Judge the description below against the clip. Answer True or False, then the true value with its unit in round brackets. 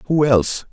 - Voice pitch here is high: False (125 Hz)